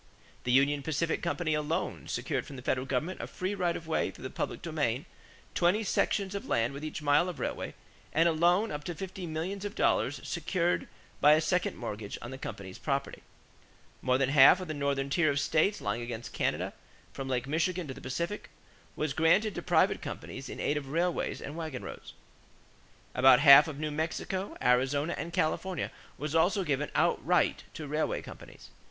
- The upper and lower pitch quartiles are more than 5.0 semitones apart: No, average, 4.1 semitones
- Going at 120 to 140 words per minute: No, average, 190 wpm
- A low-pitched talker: No, medium, 155 Hz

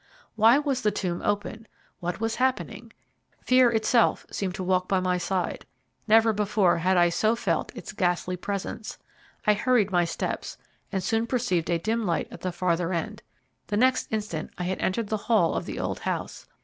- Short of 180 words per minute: No, average, 185 wpm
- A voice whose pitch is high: Yes, high, 200 Hz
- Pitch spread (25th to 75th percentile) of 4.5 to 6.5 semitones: No, average, 3.9 semitones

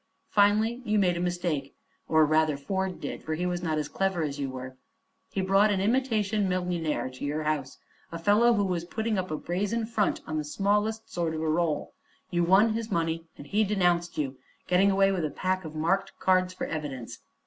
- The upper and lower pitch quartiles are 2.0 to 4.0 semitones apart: No, average, 4.4 semitones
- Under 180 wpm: No, fast, 205 wpm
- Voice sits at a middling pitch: Yes, medium, 180 Hz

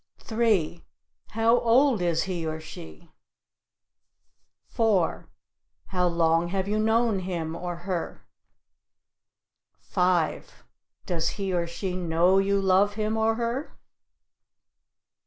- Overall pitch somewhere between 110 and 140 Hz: No, medium, 185 Hz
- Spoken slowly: Yes, slow, 105 wpm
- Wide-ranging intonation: No, average, 4.3 semitones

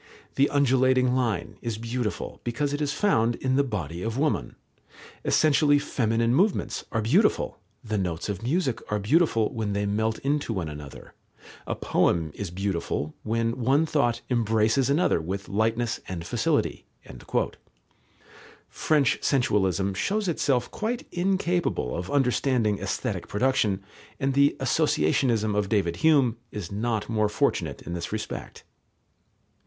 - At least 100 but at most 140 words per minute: Yes, slow, 135 wpm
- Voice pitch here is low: Yes, low, 115 Hz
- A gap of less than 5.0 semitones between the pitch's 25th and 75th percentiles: No, wide, 5.4 semitones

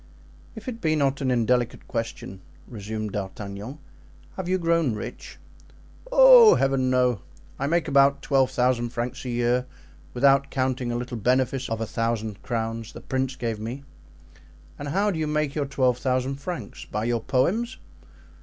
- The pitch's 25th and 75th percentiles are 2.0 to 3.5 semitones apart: Yes, average, 3.1 semitones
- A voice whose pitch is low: Yes, low, 130 Hz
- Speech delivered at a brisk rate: No, average, 160 wpm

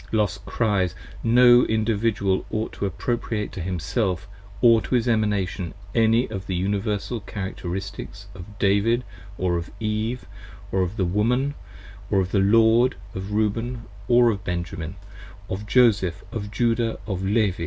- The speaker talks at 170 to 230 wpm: No, average, 145 wpm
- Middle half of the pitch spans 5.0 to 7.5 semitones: No, average, 3.2 semitones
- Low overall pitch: Yes, low, 105 Hz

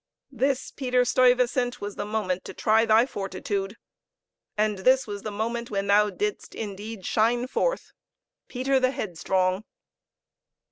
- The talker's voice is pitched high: Yes, high, 220 Hz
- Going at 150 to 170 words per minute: No, slow, 135 wpm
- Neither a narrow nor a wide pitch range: Yes, average, 3.7 semitones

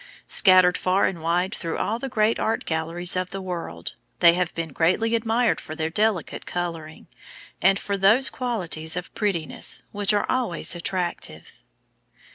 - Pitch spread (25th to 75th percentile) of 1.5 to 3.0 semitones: No, average, 4.1 semitones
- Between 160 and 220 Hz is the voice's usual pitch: Yes, medium, 185 Hz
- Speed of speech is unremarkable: Yes, average, 155 wpm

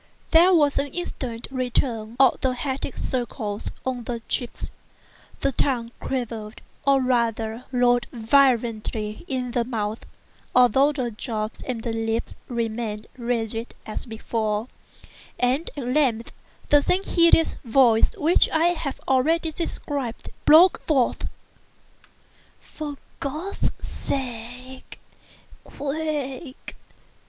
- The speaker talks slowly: Yes, slow, 105 wpm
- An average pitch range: Yes, average, 3.6 semitones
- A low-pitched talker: No, very high, 250 Hz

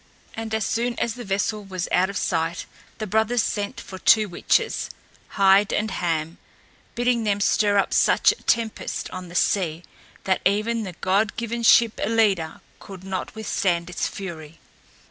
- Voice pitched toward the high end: Yes, high, 200 Hz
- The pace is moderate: Yes, average, 165 wpm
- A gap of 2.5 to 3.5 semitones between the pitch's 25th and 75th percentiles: Yes, average, 3.2 semitones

